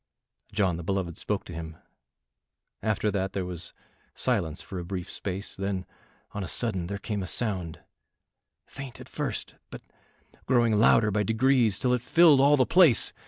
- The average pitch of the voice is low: Yes, low, 100 Hz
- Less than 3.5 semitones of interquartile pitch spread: No, average, 4.6 semitones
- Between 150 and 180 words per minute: Yes, average, 165 wpm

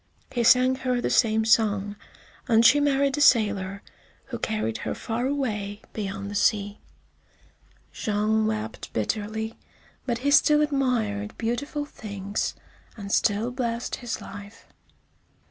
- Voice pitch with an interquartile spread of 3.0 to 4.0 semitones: Yes, average, 3.6 semitones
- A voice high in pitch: Yes, high, 220 Hz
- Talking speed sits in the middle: No, slow, 130 wpm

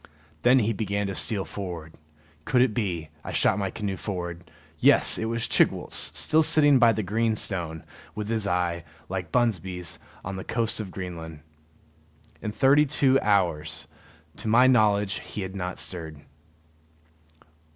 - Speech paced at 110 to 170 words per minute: Yes, average, 150 wpm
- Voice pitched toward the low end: Yes, low, 100 Hz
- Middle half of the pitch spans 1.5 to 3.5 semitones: No, average, 4.5 semitones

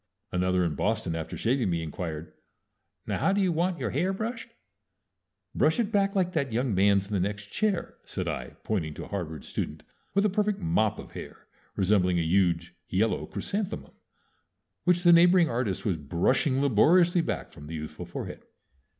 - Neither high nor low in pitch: No, low, 115 Hz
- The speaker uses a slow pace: No, average, 175 wpm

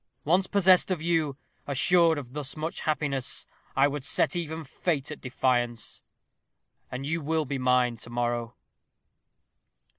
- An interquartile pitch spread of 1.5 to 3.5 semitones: No, average, 4.3 semitones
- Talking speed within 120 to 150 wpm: Yes, average, 140 wpm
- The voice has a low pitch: No, medium, 145 Hz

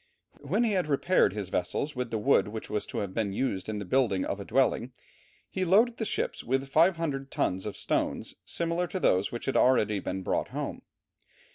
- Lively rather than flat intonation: Yes, wide, 8.4 semitones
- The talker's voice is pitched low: Yes, low, 130 Hz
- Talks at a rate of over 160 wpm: Yes, fast, 205 wpm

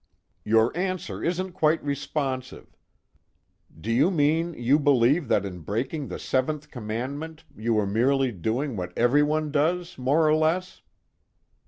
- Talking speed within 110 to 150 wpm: Yes, slow, 135 wpm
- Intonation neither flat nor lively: Yes, average, 4.9 semitones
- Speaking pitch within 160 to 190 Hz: No, medium, 140 Hz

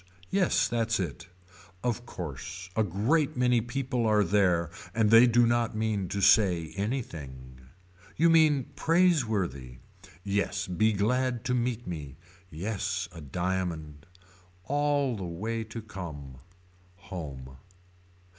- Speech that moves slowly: Yes, slow, 120 wpm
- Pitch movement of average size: No, wide, 5.8 semitones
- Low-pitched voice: Yes, low, 105 Hz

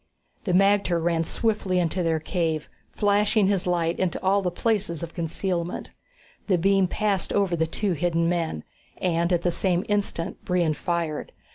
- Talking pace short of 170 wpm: Yes, average, 160 wpm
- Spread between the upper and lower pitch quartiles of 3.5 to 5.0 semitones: No, average, 2.8 semitones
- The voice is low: No, medium, 175 Hz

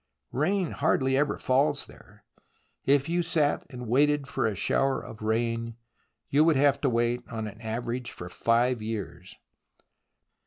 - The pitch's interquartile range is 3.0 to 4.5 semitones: Yes, average, 3.8 semitones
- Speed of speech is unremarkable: Yes, average, 150 wpm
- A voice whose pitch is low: Yes, low, 125 Hz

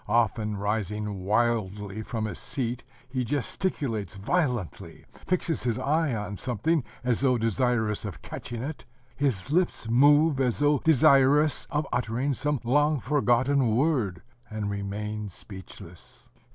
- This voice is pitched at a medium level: No, low, 120 Hz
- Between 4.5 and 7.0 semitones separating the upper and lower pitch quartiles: Yes, average, 5.1 semitones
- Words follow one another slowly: Yes, slow, 125 wpm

